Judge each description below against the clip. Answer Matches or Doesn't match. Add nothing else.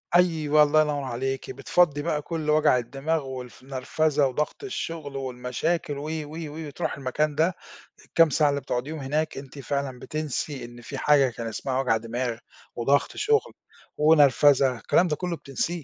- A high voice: Doesn't match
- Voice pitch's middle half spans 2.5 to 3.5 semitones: Matches